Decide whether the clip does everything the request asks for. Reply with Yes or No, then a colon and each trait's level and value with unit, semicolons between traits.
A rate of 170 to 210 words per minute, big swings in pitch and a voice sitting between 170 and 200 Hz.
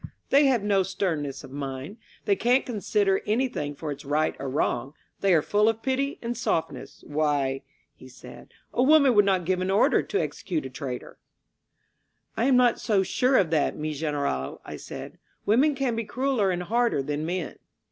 Yes: average, 190 wpm; wide, 8.2 semitones; high, 190 Hz